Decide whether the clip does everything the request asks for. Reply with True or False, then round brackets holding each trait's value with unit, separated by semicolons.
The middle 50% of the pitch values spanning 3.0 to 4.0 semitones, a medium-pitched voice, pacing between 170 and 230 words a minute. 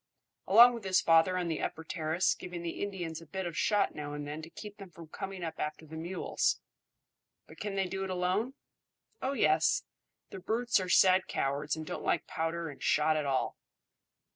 True (3.4 semitones; 175 Hz; 205 wpm)